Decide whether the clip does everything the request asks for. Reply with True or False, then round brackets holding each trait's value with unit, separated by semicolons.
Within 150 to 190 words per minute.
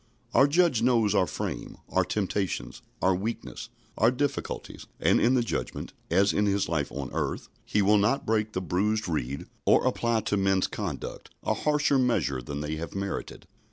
True (175 wpm)